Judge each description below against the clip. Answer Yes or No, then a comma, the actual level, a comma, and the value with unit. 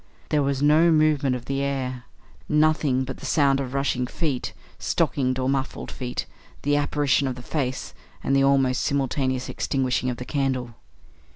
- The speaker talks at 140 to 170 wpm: Yes, average, 165 wpm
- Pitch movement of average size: No, narrow, 2.0 semitones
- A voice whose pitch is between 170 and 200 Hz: No, low, 135 Hz